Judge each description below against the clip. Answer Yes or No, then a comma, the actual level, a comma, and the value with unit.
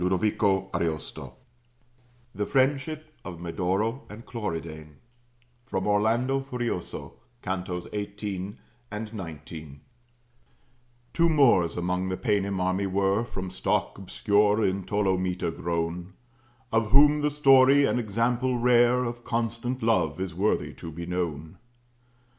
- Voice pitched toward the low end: Yes, low, 100 Hz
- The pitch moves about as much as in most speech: Yes, average, 4.8 semitones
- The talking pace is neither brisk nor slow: No, slow, 115 wpm